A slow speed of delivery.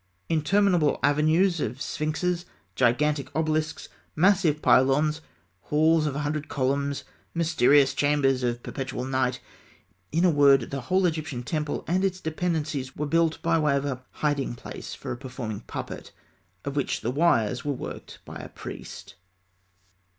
No: average, 145 wpm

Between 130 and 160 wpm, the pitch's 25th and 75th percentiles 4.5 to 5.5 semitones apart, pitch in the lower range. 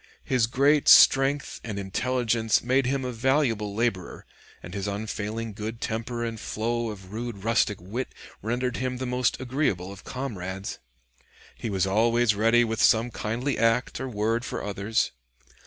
No: average, 155 wpm; average, 3.0 semitones; low, 115 Hz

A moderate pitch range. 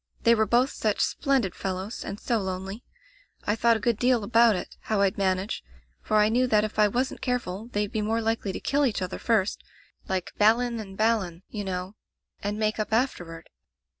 Yes: average, 3.2 semitones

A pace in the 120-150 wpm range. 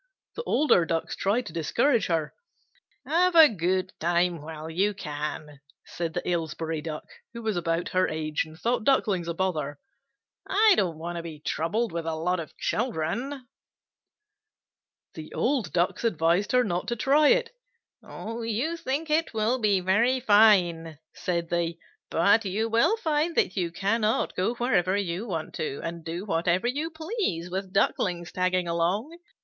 No: average, 160 wpm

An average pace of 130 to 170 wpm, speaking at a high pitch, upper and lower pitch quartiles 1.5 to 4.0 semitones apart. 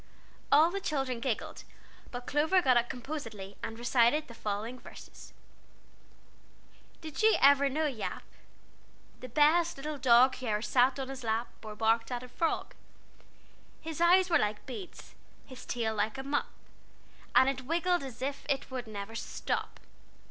No: average, 155 wpm; very high, 260 Hz; average, 4.5 semitones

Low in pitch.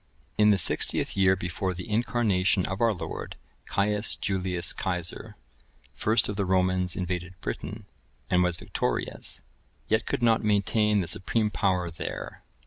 Yes: very low, 95 Hz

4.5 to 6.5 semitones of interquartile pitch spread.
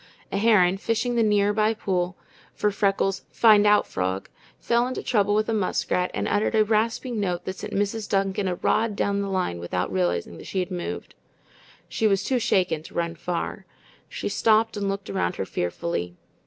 No: average, 3.2 semitones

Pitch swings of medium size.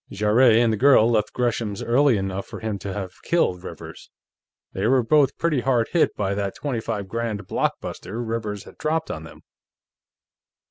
Yes: average, 3.9 semitones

